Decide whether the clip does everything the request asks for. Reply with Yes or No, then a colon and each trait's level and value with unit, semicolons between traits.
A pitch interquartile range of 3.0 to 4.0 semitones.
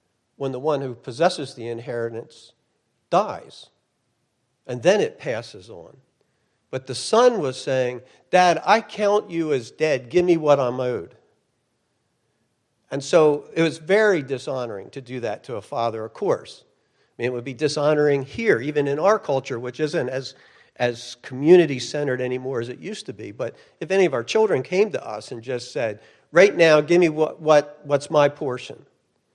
No: average, 4.7 semitones